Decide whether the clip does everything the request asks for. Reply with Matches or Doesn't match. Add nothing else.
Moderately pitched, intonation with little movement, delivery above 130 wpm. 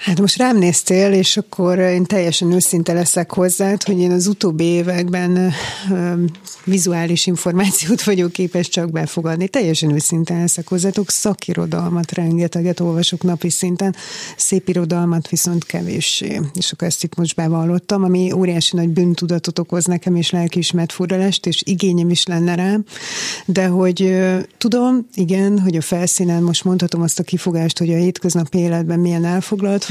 Matches